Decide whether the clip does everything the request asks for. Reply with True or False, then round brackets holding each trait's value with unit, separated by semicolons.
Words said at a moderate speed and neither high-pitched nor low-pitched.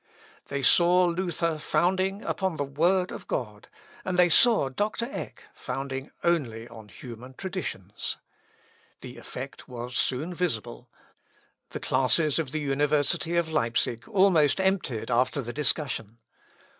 False (130 wpm; 150 Hz)